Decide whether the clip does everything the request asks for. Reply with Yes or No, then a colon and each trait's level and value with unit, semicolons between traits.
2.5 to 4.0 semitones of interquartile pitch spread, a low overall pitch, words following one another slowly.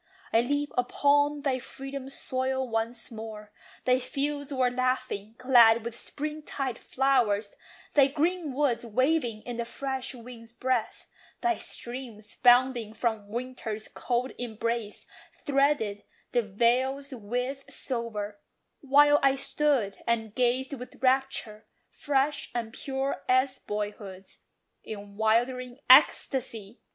No: average, 3.3 semitones; very high, 250 Hz; slow, 115 wpm